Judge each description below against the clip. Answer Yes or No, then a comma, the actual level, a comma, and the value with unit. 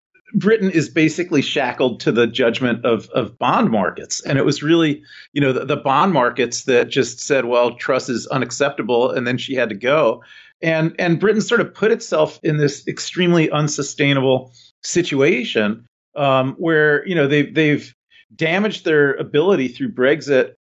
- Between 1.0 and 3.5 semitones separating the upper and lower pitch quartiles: No, average, 3.9 semitones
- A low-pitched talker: No, medium, 155 Hz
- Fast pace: No, average, 165 wpm